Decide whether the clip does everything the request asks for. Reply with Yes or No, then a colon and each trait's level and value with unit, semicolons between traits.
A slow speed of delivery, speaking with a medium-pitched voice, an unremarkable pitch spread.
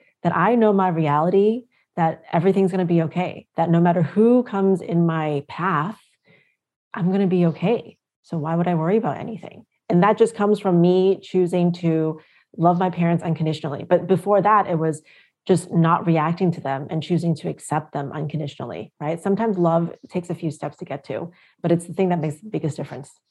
No: average, 195 wpm; medium, 175 Hz; average, 3.1 semitones